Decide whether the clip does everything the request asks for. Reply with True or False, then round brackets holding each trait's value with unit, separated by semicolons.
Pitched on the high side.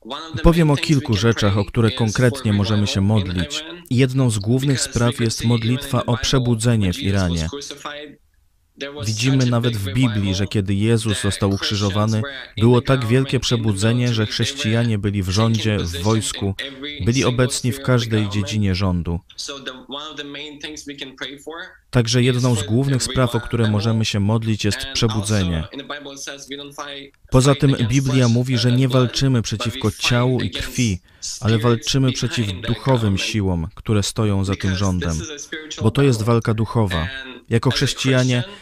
False (115 Hz)